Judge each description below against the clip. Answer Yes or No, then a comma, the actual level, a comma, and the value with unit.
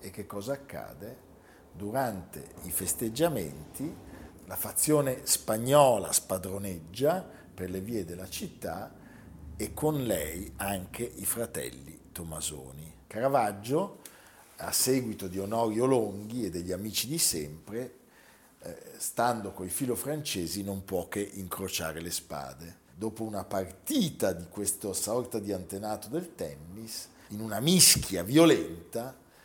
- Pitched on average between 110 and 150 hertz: No, low, 100 Hz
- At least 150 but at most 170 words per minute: No, average, 120 wpm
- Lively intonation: No, average, 4.6 semitones